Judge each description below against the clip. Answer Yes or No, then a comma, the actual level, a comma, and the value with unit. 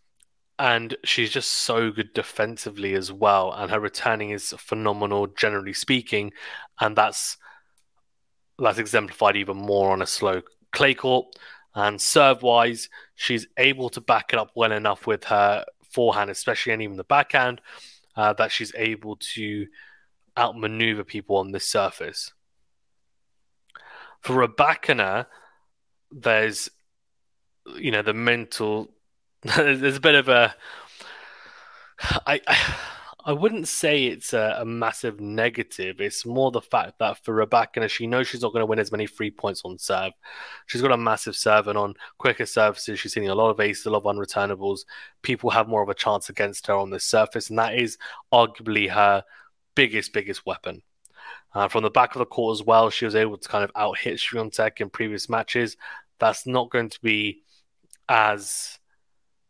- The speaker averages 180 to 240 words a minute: No, average, 165 wpm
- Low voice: Yes, low, 110 Hz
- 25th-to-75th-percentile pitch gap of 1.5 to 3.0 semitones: Yes, narrow, 2.6 semitones